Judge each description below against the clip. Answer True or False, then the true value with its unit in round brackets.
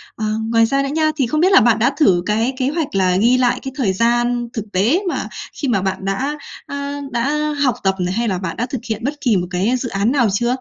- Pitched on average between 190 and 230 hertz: False (240 Hz)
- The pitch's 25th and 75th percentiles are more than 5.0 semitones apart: True (5.5 semitones)